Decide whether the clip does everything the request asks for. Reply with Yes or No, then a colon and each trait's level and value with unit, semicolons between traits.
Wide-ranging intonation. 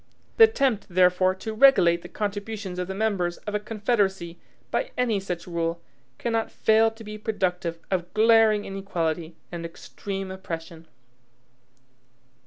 No: average, 3.8 semitones